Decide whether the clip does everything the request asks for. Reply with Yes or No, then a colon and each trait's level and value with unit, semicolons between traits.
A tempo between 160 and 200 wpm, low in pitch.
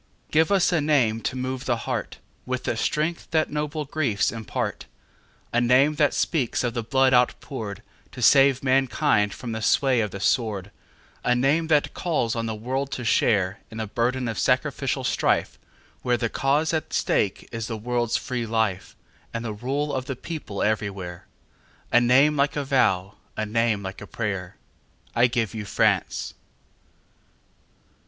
No: average, 145 wpm; low, 120 Hz